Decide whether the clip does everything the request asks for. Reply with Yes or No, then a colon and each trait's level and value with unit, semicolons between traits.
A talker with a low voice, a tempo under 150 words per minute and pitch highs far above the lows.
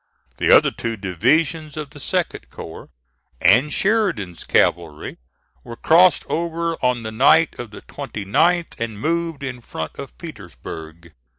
Yes: low, 125 Hz; slow, 135 wpm; wide, 8.8 semitones